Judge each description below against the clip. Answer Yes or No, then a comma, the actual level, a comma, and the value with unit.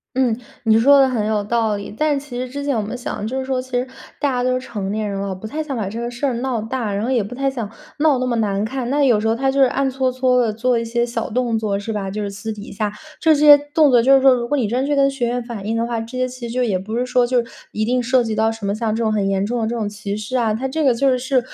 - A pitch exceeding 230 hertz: Yes, high, 240 Hz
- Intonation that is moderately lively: Yes, average, 3.2 semitones